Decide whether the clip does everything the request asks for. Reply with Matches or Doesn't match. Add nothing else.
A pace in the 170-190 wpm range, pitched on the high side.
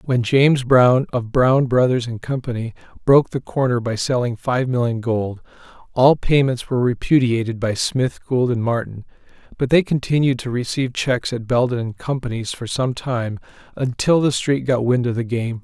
Doesn't match